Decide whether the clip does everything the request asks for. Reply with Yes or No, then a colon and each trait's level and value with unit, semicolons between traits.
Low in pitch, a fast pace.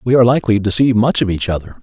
Yes: low, 115 Hz; fast, 295 wpm